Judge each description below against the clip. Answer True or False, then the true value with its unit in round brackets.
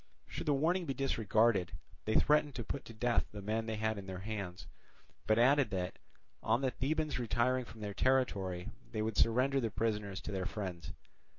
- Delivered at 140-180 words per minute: False (190 wpm)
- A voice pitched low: True (110 Hz)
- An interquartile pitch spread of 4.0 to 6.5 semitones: True (4.3 semitones)